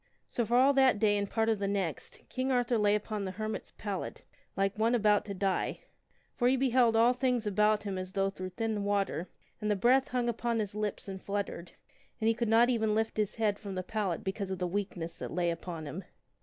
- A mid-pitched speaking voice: No, high, 210 Hz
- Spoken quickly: Yes, fast, 235 wpm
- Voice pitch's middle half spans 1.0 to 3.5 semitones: Yes, average, 2.9 semitones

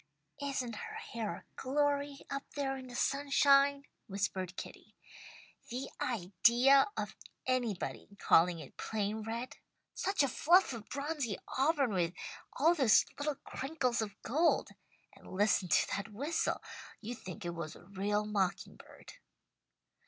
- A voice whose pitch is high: Yes, high, 245 Hz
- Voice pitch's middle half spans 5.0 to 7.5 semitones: Yes, wide, 5.5 semitones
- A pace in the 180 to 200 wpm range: No, average, 140 wpm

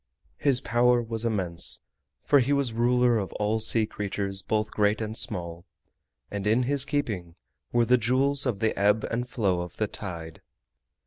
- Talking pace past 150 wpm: Yes, average, 175 wpm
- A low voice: Yes, low, 110 Hz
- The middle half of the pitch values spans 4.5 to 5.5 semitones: No, average, 3.5 semitones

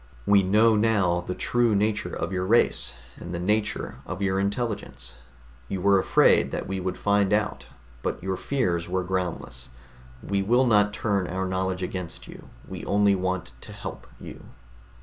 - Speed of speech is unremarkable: Yes, average, 170 wpm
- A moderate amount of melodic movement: No, narrow, 2.1 semitones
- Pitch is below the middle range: Yes, very low, 95 Hz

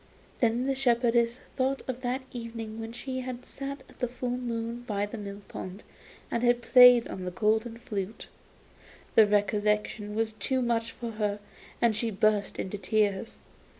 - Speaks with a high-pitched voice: Yes, high, 230 Hz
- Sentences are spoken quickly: No, average, 165 wpm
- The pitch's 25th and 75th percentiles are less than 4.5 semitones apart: Yes, average, 2.7 semitones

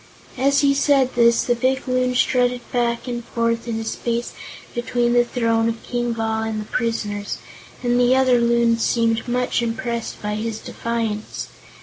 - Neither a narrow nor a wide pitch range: No, narrow, 1.4 semitones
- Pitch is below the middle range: No, high, 235 Hz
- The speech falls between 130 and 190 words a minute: Yes, average, 165 wpm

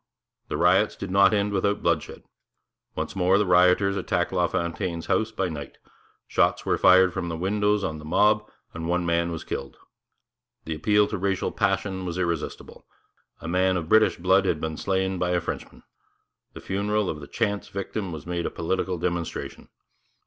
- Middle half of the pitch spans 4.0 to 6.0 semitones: No, narrow, 2.6 semitones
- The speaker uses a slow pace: No, average, 175 wpm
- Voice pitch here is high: No, very low, 90 Hz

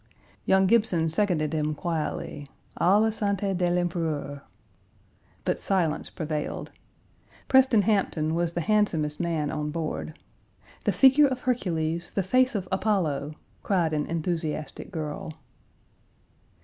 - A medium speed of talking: No, slow, 120 wpm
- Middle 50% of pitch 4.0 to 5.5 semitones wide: Yes, average, 4.5 semitones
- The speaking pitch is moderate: Yes, medium, 170 Hz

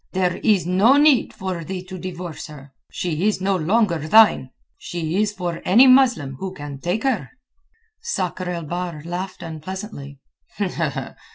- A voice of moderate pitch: Yes, medium, 180 Hz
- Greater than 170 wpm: No, average, 150 wpm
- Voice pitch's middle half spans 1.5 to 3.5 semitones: No, average, 3.9 semitones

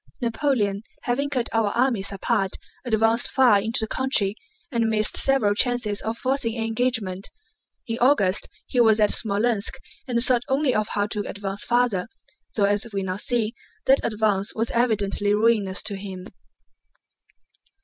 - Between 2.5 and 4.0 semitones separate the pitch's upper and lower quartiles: Yes, average, 3.1 semitones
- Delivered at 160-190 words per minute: No, average, 150 wpm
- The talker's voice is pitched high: Yes, high, 220 Hz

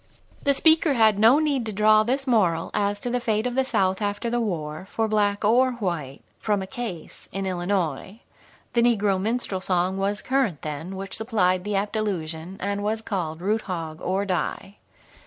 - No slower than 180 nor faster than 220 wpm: Yes, average, 190 wpm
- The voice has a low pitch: No, high, 205 Hz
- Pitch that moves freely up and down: No, average, 3.5 semitones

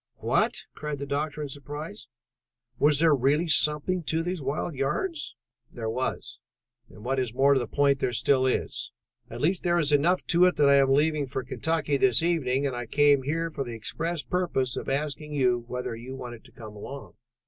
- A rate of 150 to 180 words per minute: No, average, 200 wpm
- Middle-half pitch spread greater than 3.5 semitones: No, average, 3.1 semitones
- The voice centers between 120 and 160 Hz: Yes, medium, 140 Hz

